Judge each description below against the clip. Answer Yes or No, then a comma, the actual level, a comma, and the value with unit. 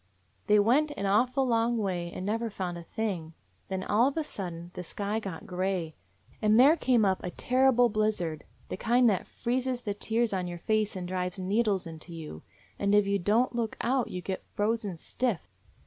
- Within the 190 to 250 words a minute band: Yes, average, 195 wpm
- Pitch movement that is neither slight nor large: Yes, average, 4.4 semitones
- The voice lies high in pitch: Yes, high, 205 Hz